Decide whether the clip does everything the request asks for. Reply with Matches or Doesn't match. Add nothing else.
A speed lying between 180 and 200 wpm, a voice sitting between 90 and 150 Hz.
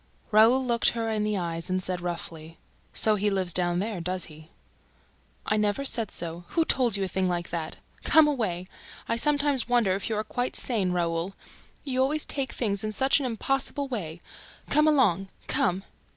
Doesn't match